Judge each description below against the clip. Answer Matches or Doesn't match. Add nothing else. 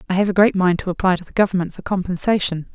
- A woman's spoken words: Matches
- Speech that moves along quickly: Matches